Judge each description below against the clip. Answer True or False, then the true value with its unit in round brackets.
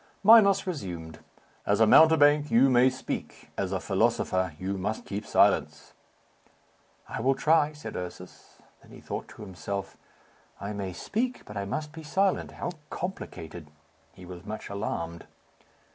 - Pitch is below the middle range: True (110 Hz)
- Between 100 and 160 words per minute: True (145 wpm)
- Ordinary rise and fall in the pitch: False (8.4 semitones)